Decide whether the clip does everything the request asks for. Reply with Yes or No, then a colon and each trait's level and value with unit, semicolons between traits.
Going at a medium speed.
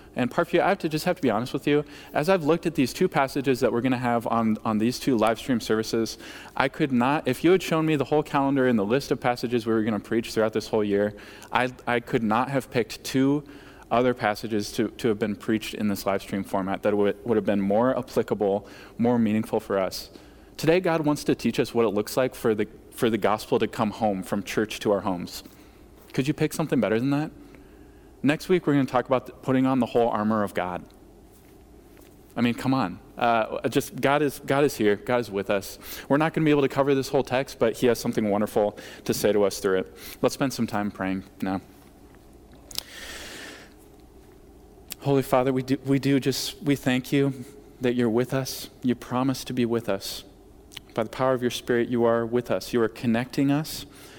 No: fast, 230 wpm